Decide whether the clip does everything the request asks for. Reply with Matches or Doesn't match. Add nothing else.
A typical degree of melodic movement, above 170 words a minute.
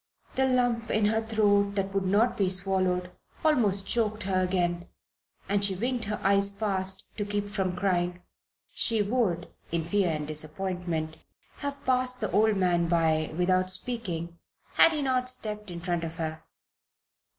Doesn't match